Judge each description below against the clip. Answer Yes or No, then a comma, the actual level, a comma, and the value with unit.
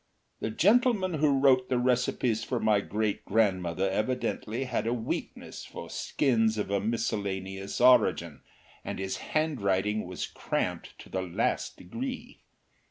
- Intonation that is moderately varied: Yes, average, 4.7 semitones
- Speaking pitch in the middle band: No, low, 110 Hz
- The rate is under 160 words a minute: Yes, slow, 135 wpm